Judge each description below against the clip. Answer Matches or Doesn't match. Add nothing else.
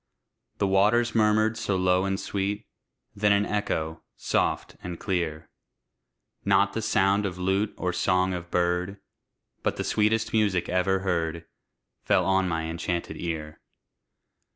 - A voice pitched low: Matches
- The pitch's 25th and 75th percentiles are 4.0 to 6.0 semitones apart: Doesn't match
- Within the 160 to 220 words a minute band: Doesn't match